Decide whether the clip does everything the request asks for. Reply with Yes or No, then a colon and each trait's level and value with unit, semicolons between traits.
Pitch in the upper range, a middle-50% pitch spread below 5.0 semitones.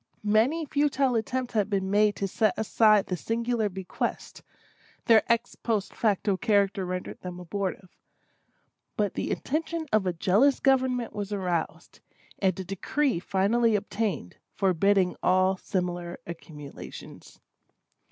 Yes: high, 205 Hz; average, 3.8 semitones